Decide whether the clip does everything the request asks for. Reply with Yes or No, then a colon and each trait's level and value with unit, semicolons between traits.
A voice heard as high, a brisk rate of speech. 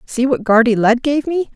Yes: very high, 250 Hz; fast, 230 wpm